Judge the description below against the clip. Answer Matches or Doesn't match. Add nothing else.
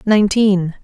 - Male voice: Doesn't match